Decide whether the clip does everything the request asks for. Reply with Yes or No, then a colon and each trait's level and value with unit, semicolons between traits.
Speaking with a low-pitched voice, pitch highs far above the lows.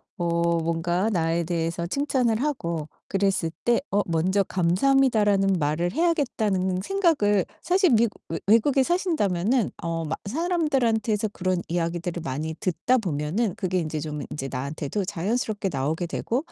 No: high, 190 Hz; wide, 5.8 semitones